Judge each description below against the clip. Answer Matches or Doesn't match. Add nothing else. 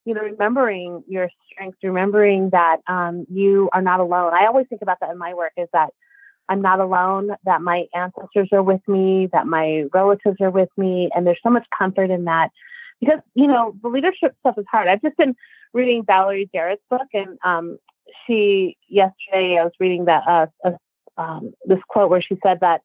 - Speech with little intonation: Doesn't match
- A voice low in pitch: Doesn't match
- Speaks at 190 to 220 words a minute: Matches